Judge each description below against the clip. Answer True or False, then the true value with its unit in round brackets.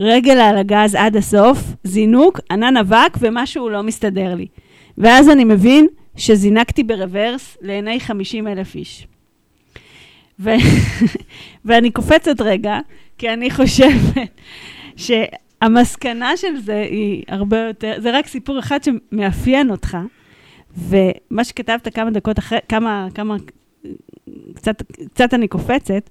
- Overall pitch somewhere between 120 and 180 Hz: False (225 Hz)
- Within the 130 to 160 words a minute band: False (115 wpm)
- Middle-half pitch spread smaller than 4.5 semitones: True (3.2 semitones)